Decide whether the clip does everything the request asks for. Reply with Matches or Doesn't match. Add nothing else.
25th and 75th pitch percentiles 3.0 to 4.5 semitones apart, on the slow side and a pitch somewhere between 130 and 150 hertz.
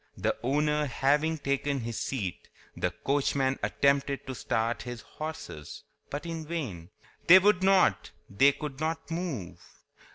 Matches